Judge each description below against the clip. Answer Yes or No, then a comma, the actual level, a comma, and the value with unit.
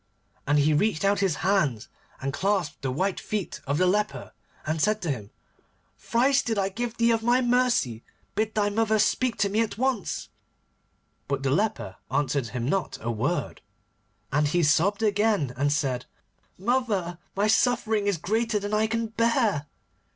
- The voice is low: No, high, 200 Hz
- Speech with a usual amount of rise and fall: No, wide, 7.1 semitones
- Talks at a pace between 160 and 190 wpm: Yes, average, 165 wpm